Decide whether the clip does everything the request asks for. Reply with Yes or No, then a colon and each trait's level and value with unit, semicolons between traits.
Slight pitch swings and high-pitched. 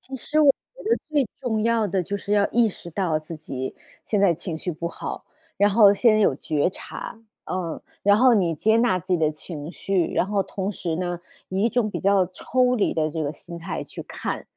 No: average, 4.6 semitones; high, 195 Hz